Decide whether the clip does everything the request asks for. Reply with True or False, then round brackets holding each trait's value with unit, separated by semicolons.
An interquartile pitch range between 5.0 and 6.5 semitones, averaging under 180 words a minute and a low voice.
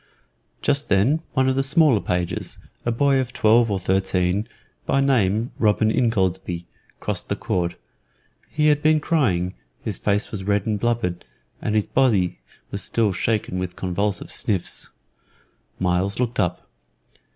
True (5.6 semitones; 145 wpm; 105 Hz)